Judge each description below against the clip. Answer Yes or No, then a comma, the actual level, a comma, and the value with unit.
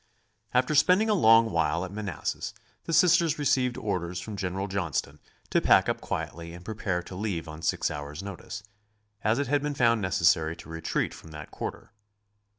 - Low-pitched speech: Yes, low, 100 Hz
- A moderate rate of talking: Yes, average, 175 wpm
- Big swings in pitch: Yes, wide, 6.7 semitones